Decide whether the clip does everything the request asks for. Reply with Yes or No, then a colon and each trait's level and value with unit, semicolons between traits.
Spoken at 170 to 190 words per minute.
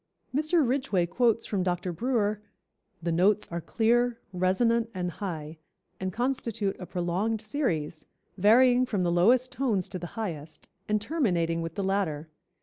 No: average, 145 wpm